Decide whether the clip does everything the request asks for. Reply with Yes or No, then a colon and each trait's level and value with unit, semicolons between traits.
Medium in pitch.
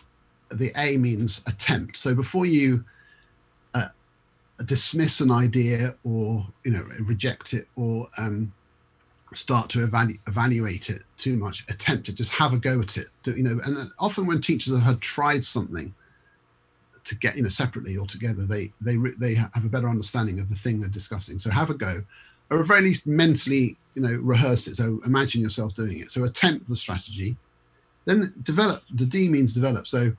No: low, 120 Hz